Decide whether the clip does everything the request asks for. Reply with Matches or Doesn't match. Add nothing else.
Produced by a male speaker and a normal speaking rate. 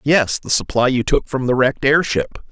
Doesn't match